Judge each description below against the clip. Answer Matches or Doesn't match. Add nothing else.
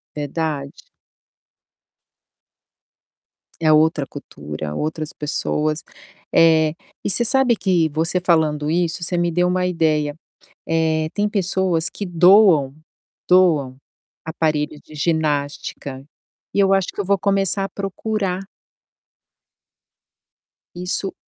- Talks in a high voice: Doesn't match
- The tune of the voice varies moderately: Matches